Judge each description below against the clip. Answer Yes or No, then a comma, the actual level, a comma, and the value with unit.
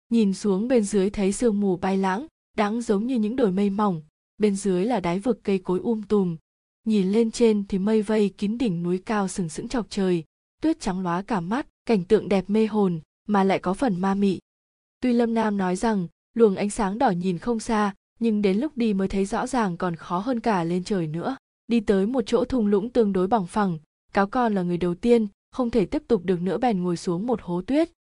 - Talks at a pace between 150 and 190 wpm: No, average, 235 wpm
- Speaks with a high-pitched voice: Yes, high, 210 Hz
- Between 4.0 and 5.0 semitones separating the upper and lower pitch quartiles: No, average, 3.6 semitones